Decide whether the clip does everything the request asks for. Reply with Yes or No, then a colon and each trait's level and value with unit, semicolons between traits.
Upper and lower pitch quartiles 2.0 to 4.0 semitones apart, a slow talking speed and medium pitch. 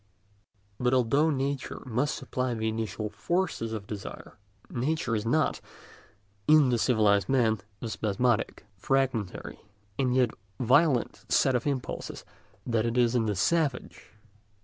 No: average, 3.4 semitones; slow, 130 wpm; low, 125 Hz